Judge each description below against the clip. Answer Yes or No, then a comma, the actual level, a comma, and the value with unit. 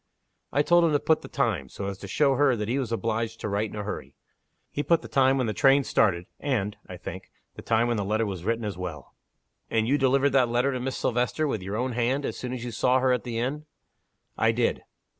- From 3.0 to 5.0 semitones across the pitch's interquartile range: Yes, average, 4.1 semitones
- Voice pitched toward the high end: No, low, 120 Hz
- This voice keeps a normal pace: No, fast, 255 wpm